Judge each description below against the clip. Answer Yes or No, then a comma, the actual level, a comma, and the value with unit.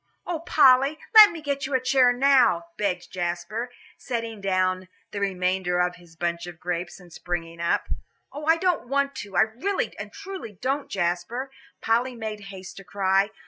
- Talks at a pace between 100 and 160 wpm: No, average, 175 wpm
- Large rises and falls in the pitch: Yes, wide, 7.3 semitones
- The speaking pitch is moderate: No, high, 210 Hz